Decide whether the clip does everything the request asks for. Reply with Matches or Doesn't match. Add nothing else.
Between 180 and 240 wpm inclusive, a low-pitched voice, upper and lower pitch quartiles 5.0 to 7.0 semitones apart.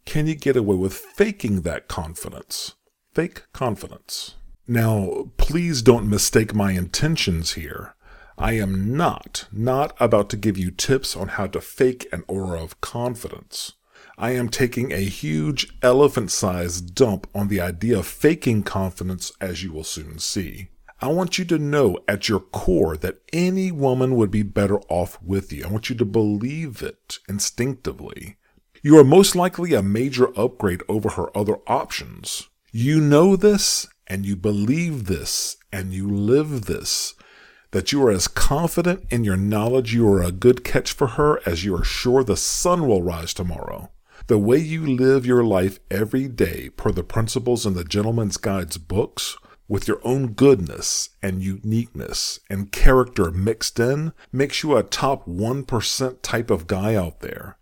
Doesn't match